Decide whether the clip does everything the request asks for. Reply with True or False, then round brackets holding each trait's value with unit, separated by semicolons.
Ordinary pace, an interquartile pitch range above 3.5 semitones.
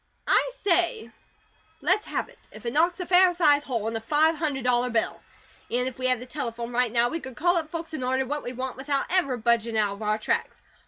False (235 wpm; 5.1 semitones)